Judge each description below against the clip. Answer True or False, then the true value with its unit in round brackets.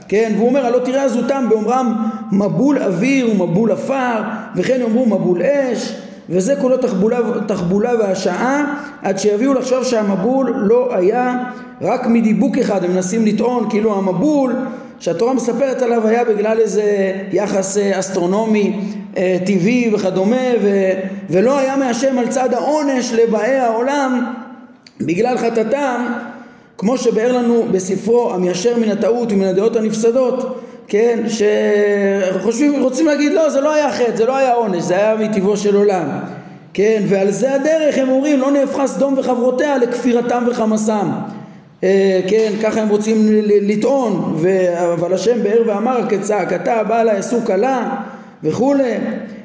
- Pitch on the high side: True (230 Hz)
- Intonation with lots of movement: False (3.8 semitones)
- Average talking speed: True (135 wpm)